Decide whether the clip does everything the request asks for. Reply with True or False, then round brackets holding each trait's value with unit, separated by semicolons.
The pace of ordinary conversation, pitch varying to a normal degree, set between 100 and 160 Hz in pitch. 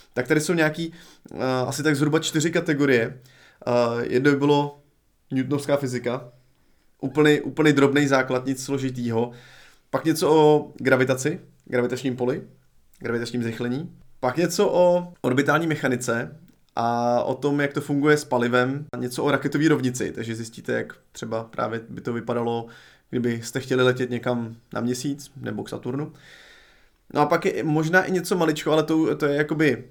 True (150 wpm; 3.5 semitones; 135 Hz)